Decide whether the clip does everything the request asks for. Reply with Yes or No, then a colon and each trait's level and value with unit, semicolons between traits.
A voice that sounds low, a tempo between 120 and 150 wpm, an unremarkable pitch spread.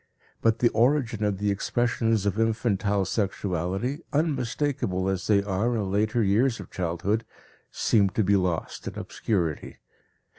Yes: low, 105 Hz; average, 140 wpm; average, 3.3 semitones